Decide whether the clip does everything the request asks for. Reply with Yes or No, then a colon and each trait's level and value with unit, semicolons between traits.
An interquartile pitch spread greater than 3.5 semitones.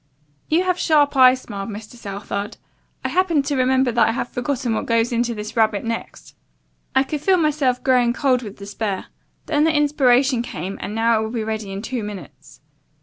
Yes: average, 4.2 semitones